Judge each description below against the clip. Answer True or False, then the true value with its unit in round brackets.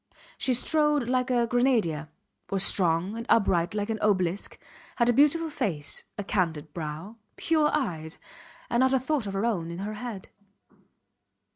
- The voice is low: False (215 Hz)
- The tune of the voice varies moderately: False (6.2 semitones)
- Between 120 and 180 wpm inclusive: True (160 wpm)